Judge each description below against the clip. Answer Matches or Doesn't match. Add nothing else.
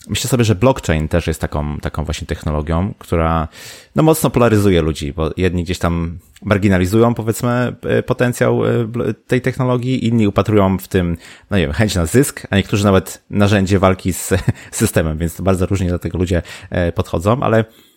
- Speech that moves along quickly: Matches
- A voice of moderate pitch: Doesn't match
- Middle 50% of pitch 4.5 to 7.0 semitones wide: Matches